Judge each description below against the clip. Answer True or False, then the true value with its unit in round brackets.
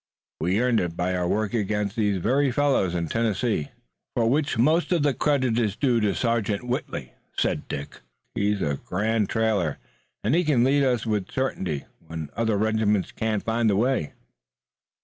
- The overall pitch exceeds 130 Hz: False (110 Hz)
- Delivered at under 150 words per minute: False (170 wpm)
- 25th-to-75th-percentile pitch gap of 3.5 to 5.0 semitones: True (4.1 semitones)